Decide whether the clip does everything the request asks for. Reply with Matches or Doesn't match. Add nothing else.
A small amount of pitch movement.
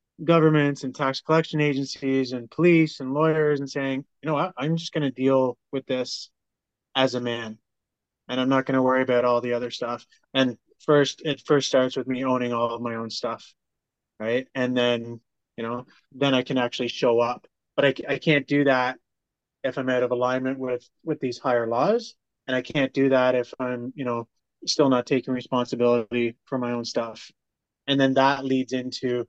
Matches